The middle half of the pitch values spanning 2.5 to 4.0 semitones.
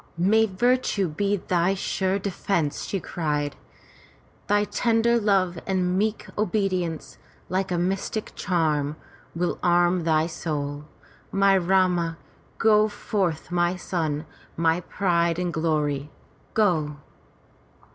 Yes: average, 3.3 semitones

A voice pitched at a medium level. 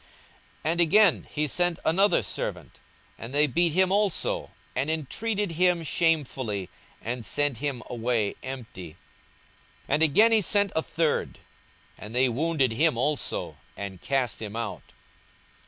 Yes: medium, 150 Hz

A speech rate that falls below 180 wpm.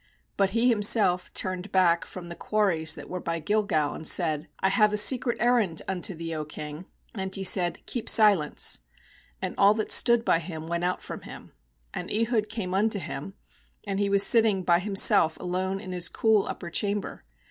No: average, 190 wpm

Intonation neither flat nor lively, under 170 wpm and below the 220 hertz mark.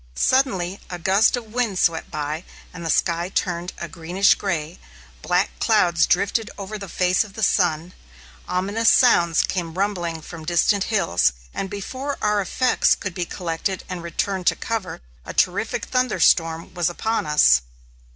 Yes: average, 3.4 semitones; average, 150 wpm; medium, 185 Hz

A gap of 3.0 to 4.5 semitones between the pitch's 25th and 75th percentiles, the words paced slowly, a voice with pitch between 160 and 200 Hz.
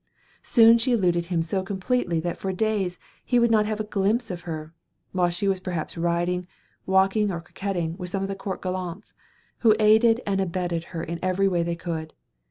No: average, 3.3 semitones; average, 195 wpm; medium, 185 Hz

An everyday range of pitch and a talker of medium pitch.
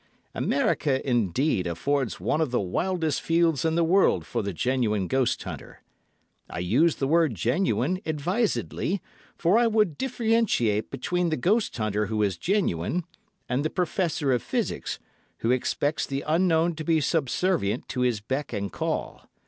No: wide, 7.1 semitones; medium, 145 Hz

